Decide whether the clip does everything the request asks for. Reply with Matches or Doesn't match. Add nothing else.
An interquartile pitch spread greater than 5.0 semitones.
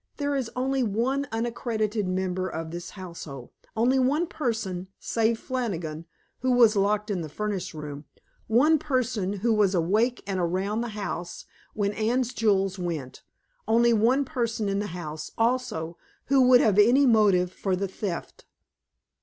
Doesn't match